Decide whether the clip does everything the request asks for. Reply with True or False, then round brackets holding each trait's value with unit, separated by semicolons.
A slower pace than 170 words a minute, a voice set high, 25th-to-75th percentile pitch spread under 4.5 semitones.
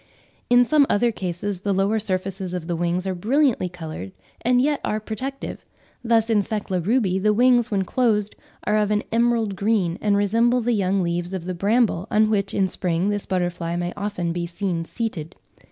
False (185 wpm; 200 Hz; 3.9 semitones)